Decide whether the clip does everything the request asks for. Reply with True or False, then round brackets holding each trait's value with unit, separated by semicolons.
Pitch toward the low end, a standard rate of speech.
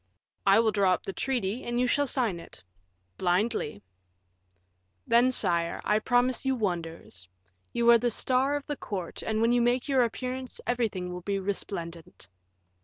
False (225 Hz; 165 wpm)